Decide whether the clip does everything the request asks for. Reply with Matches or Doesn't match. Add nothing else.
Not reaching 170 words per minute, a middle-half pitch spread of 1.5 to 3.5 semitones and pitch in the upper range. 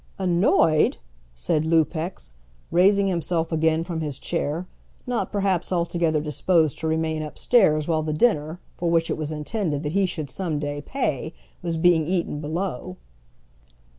Doesn't match